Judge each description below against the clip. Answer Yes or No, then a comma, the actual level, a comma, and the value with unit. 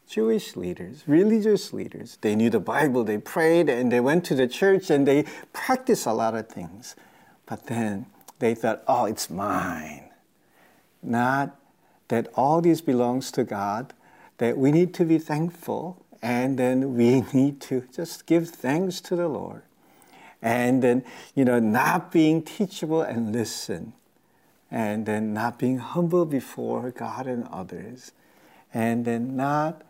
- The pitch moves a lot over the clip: Yes, wide, 6.0 semitones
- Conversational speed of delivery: Yes, average, 150 wpm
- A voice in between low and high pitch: No, low, 130 Hz